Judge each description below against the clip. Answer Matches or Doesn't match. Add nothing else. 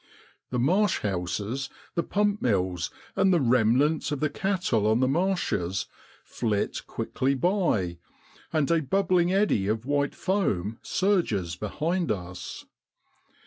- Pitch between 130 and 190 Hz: Matches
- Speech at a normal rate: Doesn't match